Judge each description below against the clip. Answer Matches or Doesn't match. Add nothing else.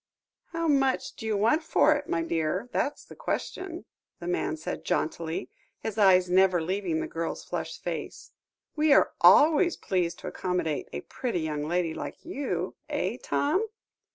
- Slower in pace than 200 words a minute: Matches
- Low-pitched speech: Doesn't match